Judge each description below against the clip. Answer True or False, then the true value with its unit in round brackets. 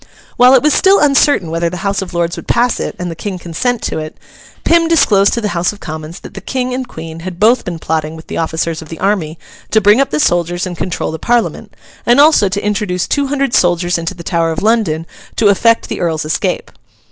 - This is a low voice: False (185 Hz)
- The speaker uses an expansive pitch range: True (6.1 semitones)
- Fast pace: True (235 wpm)